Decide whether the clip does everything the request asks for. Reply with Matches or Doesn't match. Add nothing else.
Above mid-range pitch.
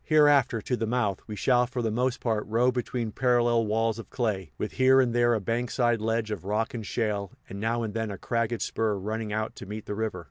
Doesn't match